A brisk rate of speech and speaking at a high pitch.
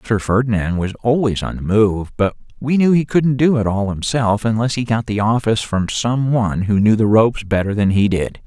No: fast, 225 wpm; low, 110 Hz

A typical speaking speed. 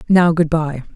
Yes: average, 190 wpm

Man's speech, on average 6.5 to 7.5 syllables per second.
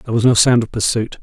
Yes: male; 6.8 syllables/s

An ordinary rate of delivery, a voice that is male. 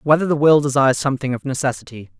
Yes: average, 190 wpm; male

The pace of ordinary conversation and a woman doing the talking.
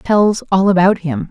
Yes: average, 185 wpm; female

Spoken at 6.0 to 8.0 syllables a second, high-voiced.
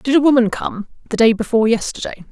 Yes: 6.5 syllables/s; high, 235 Hz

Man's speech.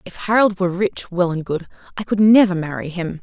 No: female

